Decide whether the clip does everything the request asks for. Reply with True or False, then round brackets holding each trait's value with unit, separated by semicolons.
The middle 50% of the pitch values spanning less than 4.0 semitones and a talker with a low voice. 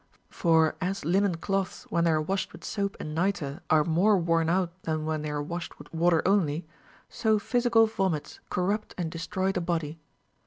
False (3.4 semitones; 175 Hz)